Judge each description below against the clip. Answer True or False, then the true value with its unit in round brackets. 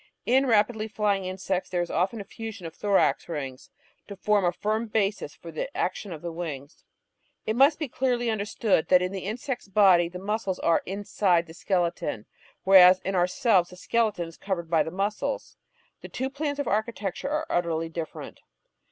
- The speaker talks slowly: False (180 wpm)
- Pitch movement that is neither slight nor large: True (3.9 semitones)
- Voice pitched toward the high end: True (195 Hz)